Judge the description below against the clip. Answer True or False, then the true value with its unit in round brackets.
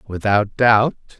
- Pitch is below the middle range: True (110 Hz)